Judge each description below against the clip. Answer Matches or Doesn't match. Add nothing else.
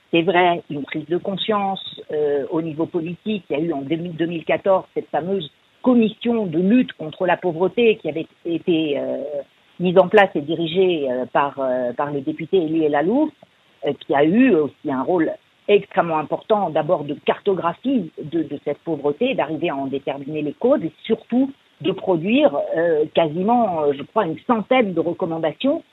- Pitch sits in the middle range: Matches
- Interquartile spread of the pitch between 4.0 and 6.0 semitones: Matches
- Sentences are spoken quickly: Doesn't match